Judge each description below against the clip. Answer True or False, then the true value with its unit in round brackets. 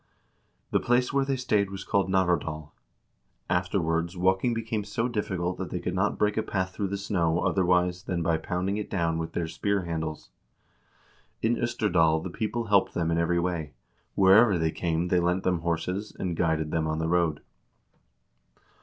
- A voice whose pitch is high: False (90 Hz)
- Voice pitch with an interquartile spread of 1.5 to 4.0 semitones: True (3.4 semitones)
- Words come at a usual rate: True (175 wpm)